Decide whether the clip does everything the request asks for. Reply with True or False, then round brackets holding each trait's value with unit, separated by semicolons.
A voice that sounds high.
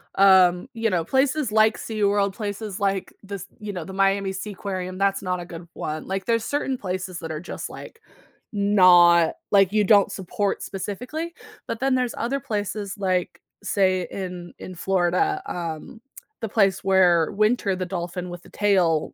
True (195 Hz)